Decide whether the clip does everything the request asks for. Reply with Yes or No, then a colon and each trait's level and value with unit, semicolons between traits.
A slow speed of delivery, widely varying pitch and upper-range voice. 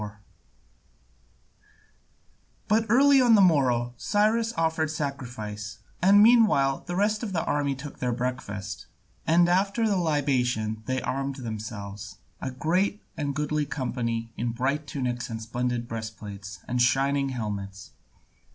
No: slow, 130 wpm; wide, 6.2 semitones; low, 135 Hz